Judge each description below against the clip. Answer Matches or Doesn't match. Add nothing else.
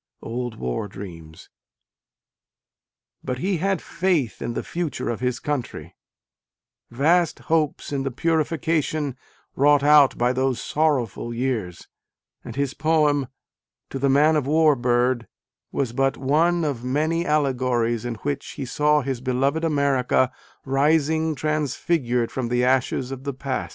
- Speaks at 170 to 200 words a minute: Doesn't match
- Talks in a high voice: Doesn't match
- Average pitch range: Matches